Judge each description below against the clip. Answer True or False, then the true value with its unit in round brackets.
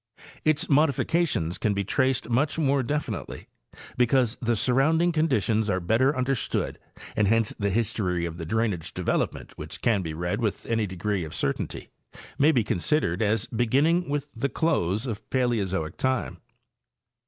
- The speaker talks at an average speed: True (155 wpm)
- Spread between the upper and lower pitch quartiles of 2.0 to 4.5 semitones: False (5.6 semitones)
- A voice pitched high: False (115 Hz)